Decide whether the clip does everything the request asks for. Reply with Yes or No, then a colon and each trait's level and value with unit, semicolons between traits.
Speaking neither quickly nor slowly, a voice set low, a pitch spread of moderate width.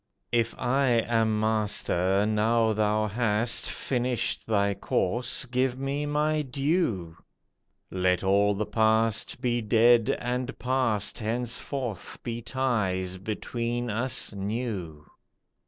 No: slow, 105 wpm; low, 115 Hz; average, 3.0 semitones